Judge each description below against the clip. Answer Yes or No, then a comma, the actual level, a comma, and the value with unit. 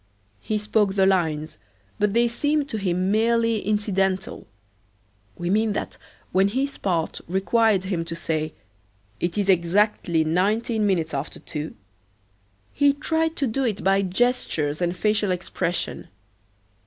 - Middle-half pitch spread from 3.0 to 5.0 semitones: Yes, average, 4.2 semitones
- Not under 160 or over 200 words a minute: No, slow, 135 wpm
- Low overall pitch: No, high, 195 Hz